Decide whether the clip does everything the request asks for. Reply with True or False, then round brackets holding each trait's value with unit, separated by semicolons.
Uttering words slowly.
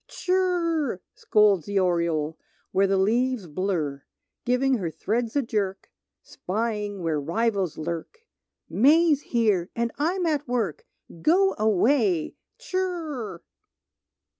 True (110 wpm)